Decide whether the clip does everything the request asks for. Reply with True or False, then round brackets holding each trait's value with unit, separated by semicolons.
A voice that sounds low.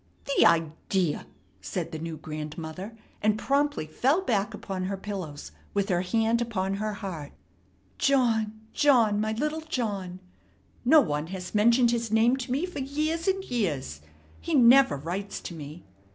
False (215 Hz)